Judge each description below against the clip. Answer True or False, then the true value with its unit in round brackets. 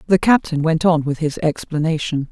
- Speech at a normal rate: True (180 wpm)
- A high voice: False (160 Hz)